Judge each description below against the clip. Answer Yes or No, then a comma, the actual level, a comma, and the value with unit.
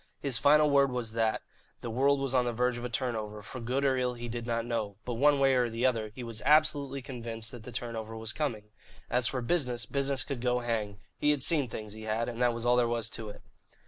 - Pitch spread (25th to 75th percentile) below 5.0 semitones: Yes, average, 2.8 semitones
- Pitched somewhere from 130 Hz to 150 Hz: No, low, 120 Hz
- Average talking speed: No, fast, 250 wpm